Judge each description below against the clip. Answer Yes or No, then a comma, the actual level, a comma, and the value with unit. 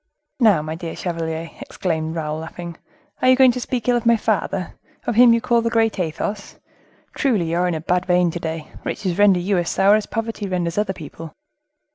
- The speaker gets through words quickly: Yes, fast, 210 wpm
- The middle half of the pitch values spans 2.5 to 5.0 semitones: No, wide, 5.4 semitones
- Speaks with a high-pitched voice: No, medium, 180 Hz